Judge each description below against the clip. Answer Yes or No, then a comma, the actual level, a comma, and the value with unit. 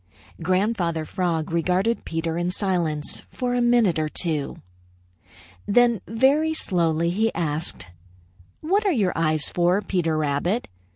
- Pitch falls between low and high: Yes, medium, 180 Hz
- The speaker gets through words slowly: Yes, slow, 125 wpm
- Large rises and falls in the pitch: Yes, wide, 5.7 semitones